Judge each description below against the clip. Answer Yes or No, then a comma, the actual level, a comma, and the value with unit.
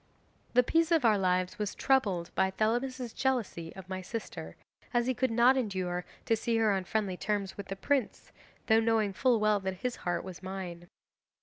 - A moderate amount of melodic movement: Yes, average, 4.2 semitones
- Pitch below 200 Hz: No, high, 210 Hz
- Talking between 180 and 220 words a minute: Yes, average, 190 wpm